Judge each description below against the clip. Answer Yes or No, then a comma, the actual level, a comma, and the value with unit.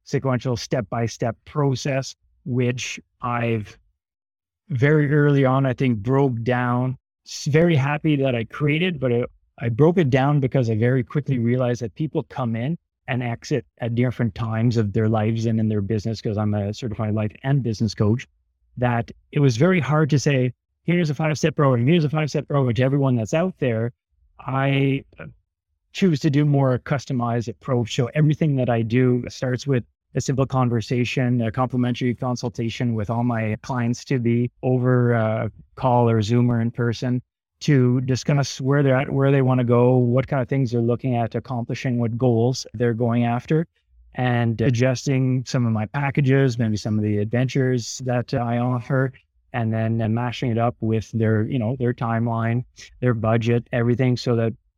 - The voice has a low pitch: Yes, low, 125 Hz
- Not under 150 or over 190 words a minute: Yes, average, 180 wpm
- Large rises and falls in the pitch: No, average, 2.7 semitones